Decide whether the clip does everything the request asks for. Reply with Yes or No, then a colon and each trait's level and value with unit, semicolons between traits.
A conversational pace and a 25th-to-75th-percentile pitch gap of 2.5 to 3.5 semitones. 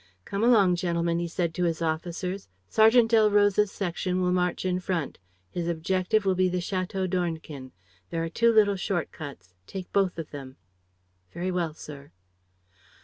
Yes: average, 160 wpm; average, 2.8 semitones